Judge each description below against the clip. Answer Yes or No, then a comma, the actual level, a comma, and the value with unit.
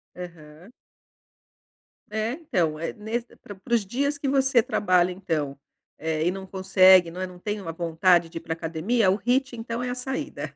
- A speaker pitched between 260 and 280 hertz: No, high, 190 Hz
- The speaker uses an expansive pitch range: Yes, wide, 6.0 semitones